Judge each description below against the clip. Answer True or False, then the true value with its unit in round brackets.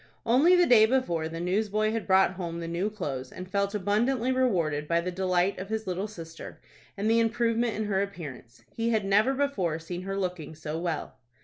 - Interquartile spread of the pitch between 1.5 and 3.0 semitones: False (4.6 semitones)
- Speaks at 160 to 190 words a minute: False (200 wpm)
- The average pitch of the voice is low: False (195 Hz)